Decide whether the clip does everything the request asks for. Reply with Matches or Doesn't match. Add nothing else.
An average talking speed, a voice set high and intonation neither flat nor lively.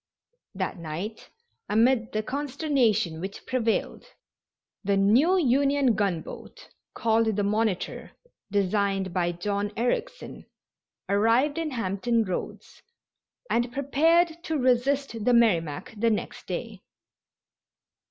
Doesn't match